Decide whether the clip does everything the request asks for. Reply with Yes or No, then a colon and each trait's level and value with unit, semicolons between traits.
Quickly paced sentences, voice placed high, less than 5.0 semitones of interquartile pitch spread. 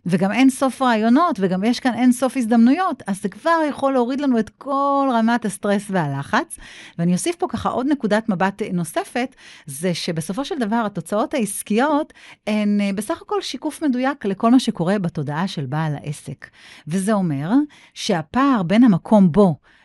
No: fast, 160 wpm; high, 220 Hz; wide, 5.5 semitones